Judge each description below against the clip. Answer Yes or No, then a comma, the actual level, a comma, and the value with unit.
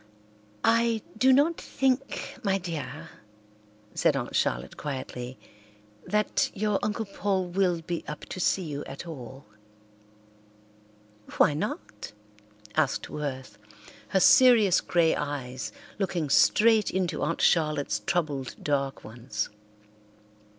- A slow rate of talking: Yes, slow, 110 wpm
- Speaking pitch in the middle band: Yes, medium, 165 Hz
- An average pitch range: No, wide, 6.6 semitones